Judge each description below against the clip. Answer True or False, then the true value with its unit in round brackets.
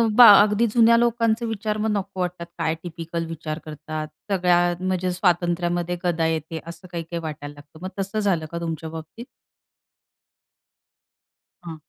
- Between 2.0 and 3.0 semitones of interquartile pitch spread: False (3.4 semitones)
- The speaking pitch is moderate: True (175 Hz)